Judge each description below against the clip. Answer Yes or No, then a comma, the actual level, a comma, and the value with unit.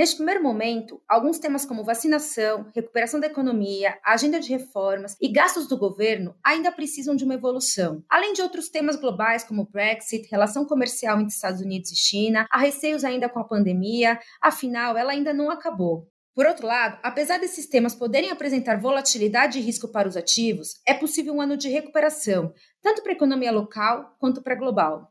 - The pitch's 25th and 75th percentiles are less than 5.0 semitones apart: No, wide, 5.4 semitones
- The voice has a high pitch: Yes, high, 245 Hz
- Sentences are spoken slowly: No, average, 180 wpm